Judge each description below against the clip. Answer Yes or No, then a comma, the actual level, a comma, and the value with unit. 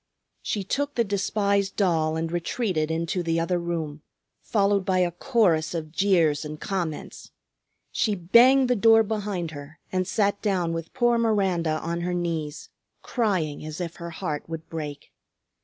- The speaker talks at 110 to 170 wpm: Yes, average, 155 wpm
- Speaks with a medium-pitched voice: Yes, medium, 175 Hz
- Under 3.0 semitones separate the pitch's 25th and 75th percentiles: No, average, 3.9 semitones